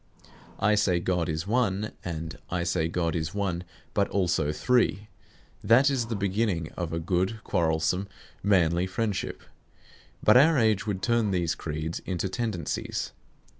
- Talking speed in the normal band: Yes, average, 145 wpm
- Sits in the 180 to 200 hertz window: No, very low, 95 Hz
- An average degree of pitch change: Yes, average, 4.2 semitones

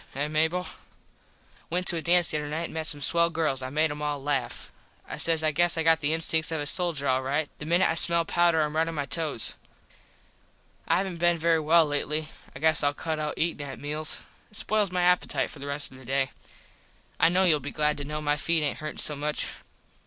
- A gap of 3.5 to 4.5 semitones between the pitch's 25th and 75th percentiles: No, narrow, 2.4 semitones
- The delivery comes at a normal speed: No, fast, 235 wpm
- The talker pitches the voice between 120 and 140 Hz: No, medium, 155 Hz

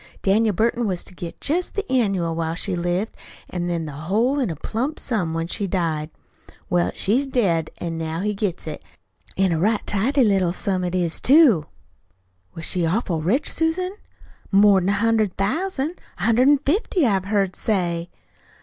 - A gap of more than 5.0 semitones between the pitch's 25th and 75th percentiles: Yes, wide, 5.4 semitones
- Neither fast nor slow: Yes, average, 175 wpm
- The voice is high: Yes, high, 195 Hz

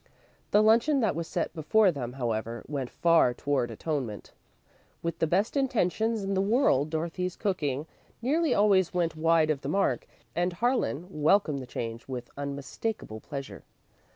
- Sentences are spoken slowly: No, average, 155 wpm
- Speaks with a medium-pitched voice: Yes, medium, 165 Hz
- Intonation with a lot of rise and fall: Yes, wide, 6.6 semitones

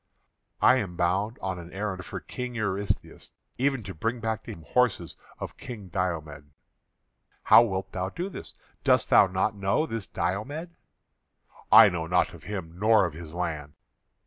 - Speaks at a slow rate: No, average, 165 wpm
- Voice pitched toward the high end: No, very low, 95 Hz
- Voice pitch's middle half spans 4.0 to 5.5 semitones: Yes, average, 4.4 semitones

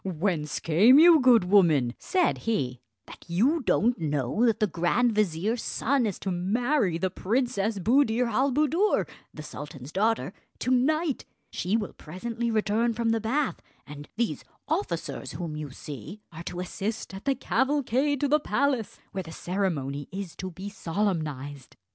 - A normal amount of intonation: No, wide, 6.6 semitones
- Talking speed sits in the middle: Yes, average, 160 wpm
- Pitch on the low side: No, high, 210 Hz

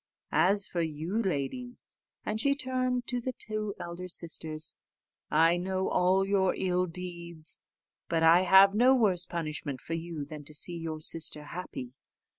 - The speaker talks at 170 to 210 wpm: No, average, 155 wpm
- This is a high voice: No, medium, 180 Hz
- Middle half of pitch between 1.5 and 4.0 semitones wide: Yes, average, 3.7 semitones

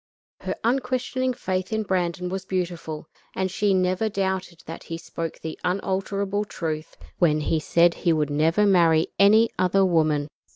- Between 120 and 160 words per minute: Yes, average, 155 wpm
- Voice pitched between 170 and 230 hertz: Yes, medium, 185 Hz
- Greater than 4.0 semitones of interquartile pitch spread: No, average, 3.2 semitones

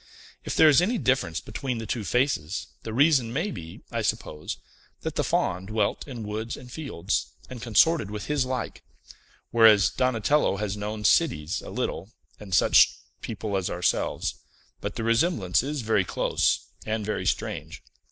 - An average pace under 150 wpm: No, average, 160 wpm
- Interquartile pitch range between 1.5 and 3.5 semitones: No, average, 4.5 semitones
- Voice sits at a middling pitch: No, low, 110 Hz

